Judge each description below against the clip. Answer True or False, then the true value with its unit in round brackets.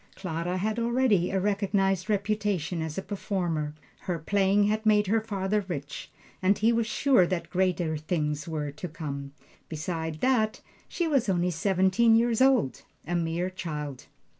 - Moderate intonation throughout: True (4.6 semitones)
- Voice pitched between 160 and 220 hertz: True (190 Hz)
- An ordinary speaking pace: True (155 wpm)